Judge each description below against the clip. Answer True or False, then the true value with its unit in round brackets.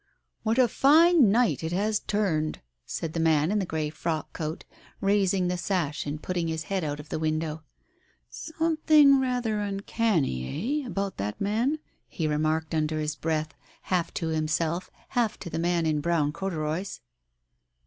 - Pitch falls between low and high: True (170 Hz)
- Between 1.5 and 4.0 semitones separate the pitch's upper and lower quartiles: False (5.2 semitones)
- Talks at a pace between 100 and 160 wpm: False (170 wpm)